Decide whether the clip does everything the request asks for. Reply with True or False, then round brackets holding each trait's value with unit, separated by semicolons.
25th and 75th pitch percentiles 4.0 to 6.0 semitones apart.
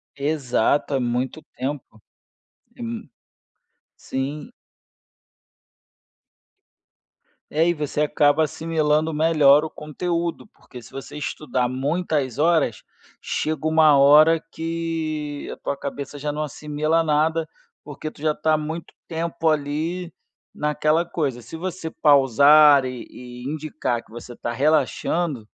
False (2.5 semitones)